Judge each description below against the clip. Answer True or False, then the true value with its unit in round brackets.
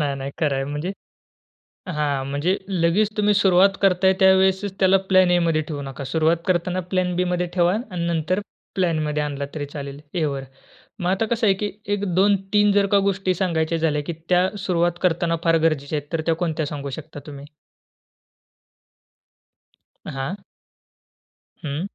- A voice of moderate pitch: True (175 Hz)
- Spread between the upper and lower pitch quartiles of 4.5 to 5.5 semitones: False (4.0 semitones)